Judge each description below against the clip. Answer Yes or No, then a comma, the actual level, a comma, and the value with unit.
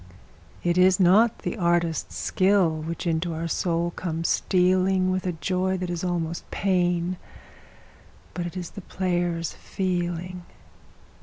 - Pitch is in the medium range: Yes, medium, 175 Hz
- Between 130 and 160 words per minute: Yes, slow, 135 wpm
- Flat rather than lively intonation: Yes, narrow, 1.5 semitones